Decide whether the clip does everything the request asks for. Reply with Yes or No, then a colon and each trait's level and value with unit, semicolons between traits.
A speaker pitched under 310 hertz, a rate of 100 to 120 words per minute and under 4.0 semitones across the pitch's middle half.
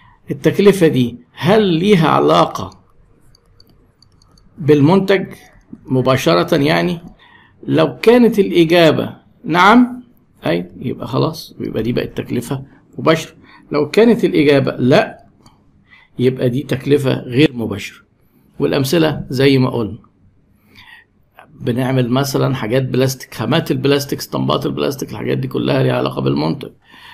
No: medium, 140 Hz; average, 105 wpm; average, 5.0 semitones